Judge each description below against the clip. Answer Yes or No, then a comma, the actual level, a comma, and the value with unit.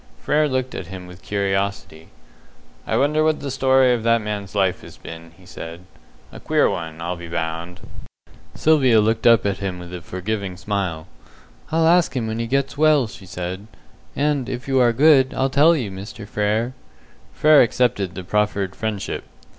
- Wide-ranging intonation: Yes, wide, 6.1 semitones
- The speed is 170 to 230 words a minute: Yes, average, 180 wpm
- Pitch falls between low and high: No, low, 105 Hz